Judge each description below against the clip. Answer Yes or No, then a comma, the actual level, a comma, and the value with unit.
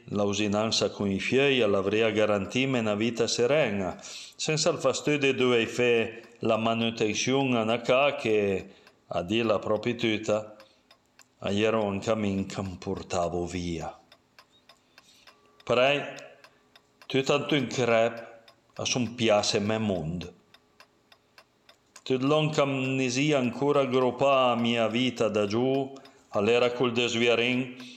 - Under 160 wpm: Yes, average, 125 wpm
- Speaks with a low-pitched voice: Yes, low, 115 Hz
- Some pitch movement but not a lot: Yes, average, 3.5 semitones